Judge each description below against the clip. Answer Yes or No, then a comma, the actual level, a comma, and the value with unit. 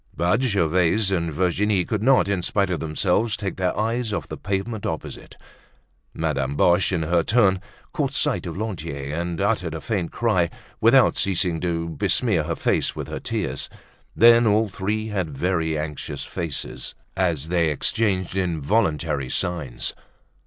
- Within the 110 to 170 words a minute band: Yes, average, 150 wpm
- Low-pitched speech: Yes, very low, 90 Hz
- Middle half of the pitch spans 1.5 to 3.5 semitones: No, average, 4.2 semitones